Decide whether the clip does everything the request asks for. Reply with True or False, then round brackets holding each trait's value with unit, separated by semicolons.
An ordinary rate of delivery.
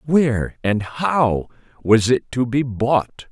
True (145 wpm)